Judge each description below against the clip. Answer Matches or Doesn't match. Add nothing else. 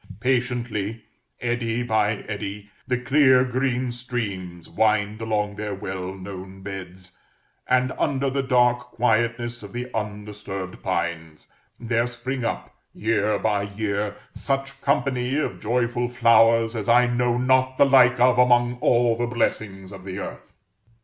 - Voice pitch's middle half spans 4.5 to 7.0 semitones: Doesn't match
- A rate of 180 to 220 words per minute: Doesn't match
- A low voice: Matches